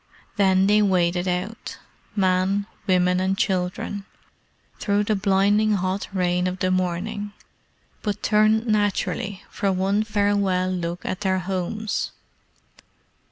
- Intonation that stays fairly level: Yes, narrow, 2.0 semitones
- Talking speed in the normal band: No, slow, 115 wpm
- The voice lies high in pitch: Yes, high, 195 Hz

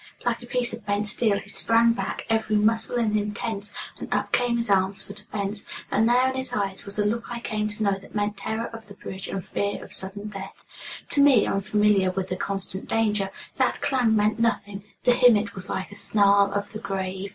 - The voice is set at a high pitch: Yes, high, 210 Hz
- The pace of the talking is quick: Yes, fast, 225 wpm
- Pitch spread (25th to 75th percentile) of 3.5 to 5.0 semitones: No, narrow, 2.4 semitones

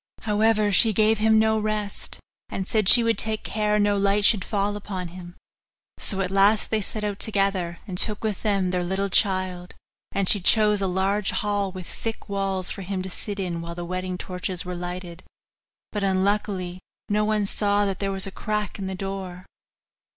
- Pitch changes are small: Yes, narrow, 2.2 semitones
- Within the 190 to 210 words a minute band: Yes, average, 195 wpm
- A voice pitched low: No, high, 195 Hz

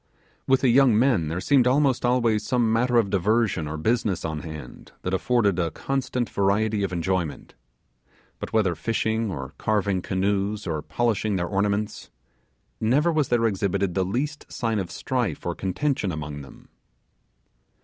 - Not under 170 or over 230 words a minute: No, average, 155 wpm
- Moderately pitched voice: No, low, 105 Hz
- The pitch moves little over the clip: No, average, 4.6 semitones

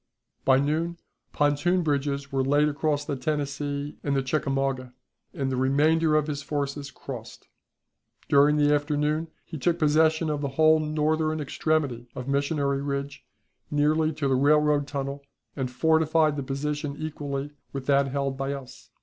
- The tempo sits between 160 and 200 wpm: No, average, 150 wpm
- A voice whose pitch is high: No, medium, 145 Hz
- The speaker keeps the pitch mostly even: Yes, narrow, 1.8 semitones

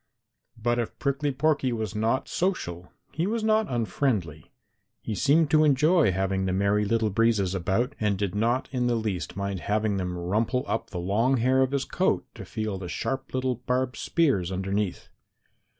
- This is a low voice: Yes, low, 115 Hz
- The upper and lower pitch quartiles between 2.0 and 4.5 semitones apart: No, average, 5.3 semitones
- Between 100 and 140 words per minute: No, average, 175 wpm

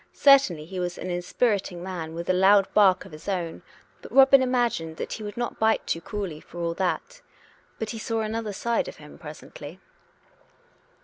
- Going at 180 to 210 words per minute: Yes, average, 185 wpm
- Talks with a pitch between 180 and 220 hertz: Yes, high, 190 Hz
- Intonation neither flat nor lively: Yes, average, 4.6 semitones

